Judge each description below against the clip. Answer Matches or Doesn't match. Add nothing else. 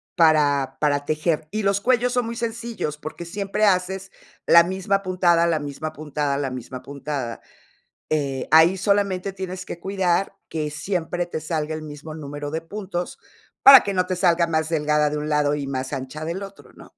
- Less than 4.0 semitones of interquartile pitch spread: Doesn't match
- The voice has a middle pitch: Matches